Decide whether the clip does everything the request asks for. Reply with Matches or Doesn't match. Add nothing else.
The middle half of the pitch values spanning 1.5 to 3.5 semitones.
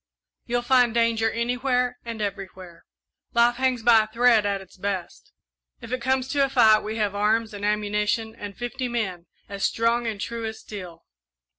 Matches